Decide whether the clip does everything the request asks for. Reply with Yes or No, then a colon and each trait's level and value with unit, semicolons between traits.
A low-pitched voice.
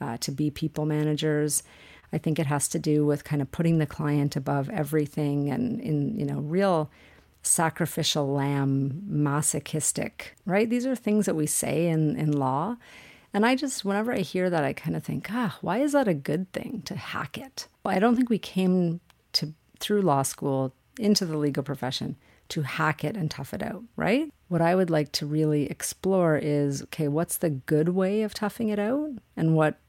No: medium, 160 Hz